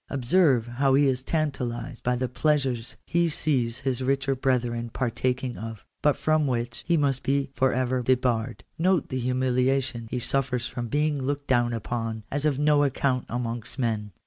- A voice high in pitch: No, low, 130 Hz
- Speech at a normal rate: Yes, average, 170 wpm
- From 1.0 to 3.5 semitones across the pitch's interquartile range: Yes, narrow, 2.6 semitones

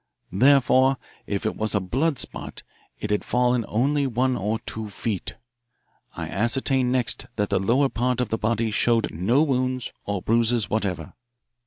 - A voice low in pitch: Yes, low, 115 Hz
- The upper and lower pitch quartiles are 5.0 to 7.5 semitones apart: No, average, 3.4 semitones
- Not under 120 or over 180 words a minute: Yes, average, 160 wpm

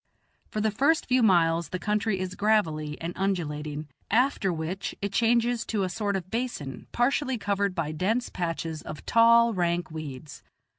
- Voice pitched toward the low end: No, high, 195 Hz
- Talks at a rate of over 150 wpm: Yes, average, 160 wpm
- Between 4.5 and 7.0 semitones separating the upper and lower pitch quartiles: Yes, wide, 5.6 semitones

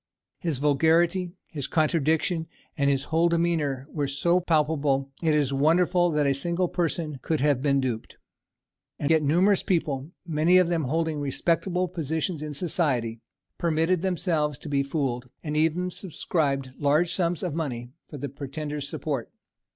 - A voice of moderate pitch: Yes, medium, 155 Hz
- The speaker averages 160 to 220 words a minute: No, average, 150 wpm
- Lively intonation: No, average, 3.3 semitones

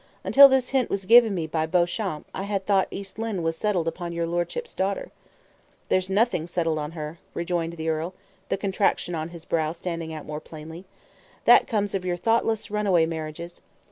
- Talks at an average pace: Yes, average, 185 wpm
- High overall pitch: No, medium, 175 Hz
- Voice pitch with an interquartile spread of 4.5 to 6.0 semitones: No, average, 3.5 semitones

